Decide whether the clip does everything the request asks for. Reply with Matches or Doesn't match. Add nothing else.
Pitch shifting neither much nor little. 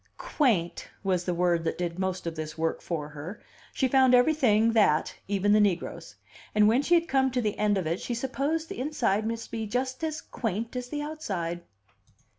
Doesn't match